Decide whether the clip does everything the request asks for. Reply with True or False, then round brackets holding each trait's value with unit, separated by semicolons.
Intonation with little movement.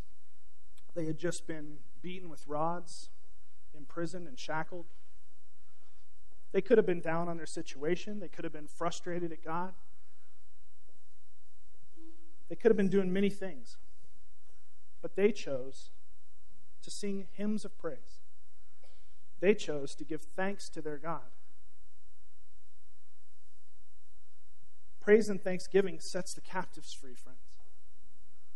False (3.7 semitones)